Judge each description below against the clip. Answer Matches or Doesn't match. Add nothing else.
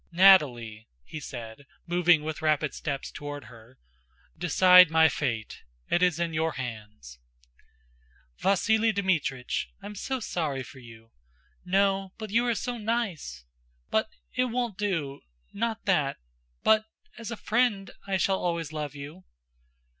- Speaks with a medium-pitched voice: Matches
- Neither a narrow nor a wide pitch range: Doesn't match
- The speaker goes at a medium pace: Doesn't match